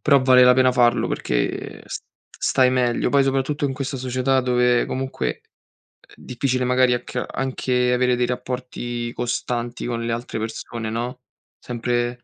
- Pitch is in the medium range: No, low, 125 Hz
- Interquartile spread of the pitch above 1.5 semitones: No, narrow, 1.2 semitones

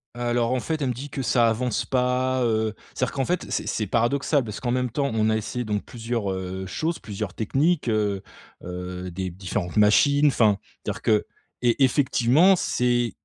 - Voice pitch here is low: Yes, low, 120 Hz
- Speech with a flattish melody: No, average, 3.6 semitones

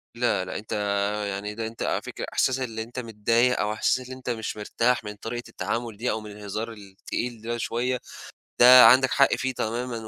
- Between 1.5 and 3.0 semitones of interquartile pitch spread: Yes, narrow, 2.5 semitones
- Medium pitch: No, low, 115 Hz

